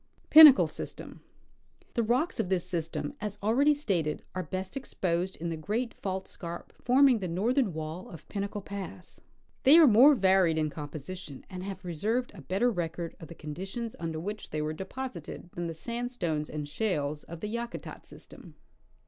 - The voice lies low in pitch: No, medium, 185 Hz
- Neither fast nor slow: Yes, average, 170 wpm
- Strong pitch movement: Yes, wide, 6.0 semitones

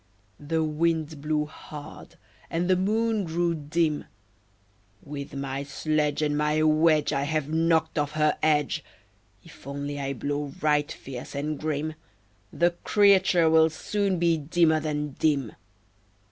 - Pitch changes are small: Yes, narrow, 2.0 semitones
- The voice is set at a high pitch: No, medium, 155 Hz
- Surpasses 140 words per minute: No, slow, 135 wpm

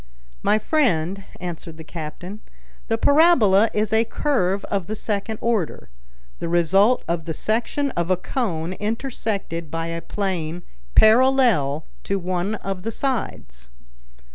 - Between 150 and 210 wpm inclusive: No, slow, 135 wpm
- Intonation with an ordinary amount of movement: Yes, average, 5.0 semitones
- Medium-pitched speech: No, high, 195 Hz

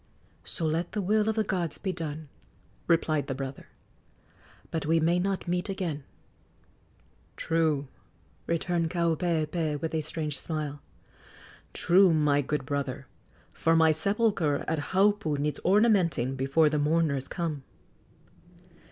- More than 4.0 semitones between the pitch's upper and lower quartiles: No, average, 3.2 semitones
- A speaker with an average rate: No, slow, 125 wpm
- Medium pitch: Yes, medium, 160 Hz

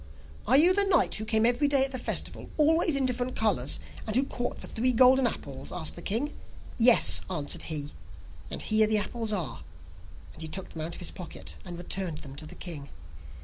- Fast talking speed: Yes, fast, 210 wpm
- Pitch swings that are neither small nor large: No, wide, 7.2 semitones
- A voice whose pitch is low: No, high, 220 Hz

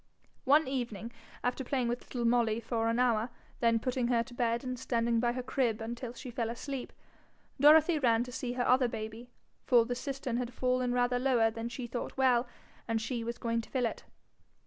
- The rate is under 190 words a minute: No, fast, 205 wpm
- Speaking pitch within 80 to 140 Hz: No, high, 245 Hz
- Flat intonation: Yes, narrow, 1.6 semitones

